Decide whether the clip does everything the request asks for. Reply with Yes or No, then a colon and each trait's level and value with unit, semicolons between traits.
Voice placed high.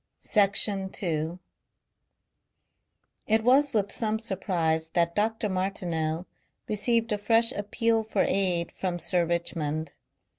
Yes: high, 195 Hz